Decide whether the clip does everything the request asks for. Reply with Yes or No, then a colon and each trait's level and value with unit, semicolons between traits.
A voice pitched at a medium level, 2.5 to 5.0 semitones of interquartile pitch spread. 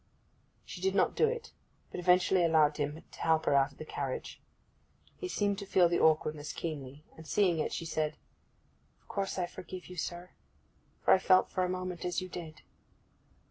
Yes: medium, 175 Hz; average, 3.0 semitones